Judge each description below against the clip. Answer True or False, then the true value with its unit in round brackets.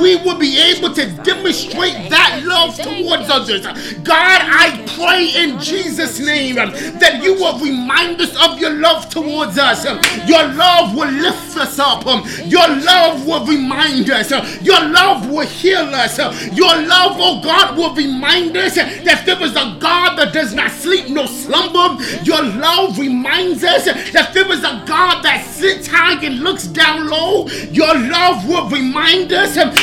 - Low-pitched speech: False (330 Hz)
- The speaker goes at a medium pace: True (165 wpm)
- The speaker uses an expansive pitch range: False (2.9 semitones)